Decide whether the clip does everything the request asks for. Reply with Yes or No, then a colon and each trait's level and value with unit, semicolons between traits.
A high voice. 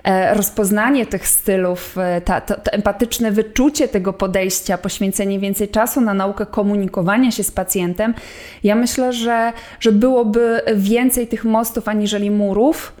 Yes: high, 210 Hz